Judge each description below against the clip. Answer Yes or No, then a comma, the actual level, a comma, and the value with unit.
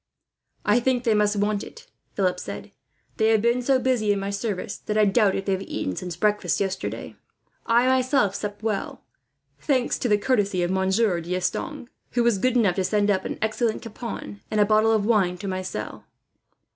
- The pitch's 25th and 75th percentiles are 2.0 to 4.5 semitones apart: Yes, average, 3.3 semitones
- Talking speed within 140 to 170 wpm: No, average, 195 wpm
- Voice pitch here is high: Yes, high, 210 Hz